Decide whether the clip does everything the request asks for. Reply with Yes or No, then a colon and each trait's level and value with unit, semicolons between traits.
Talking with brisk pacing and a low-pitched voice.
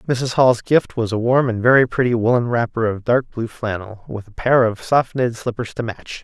Yes: fast, 230 wpm; low, 120 Hz